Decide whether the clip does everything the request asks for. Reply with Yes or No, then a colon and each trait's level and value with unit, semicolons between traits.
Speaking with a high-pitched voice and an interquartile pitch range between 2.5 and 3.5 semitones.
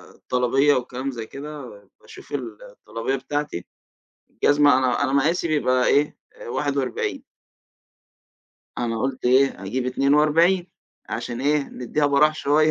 No: medium, 140 Hz; average, 2.8 semitones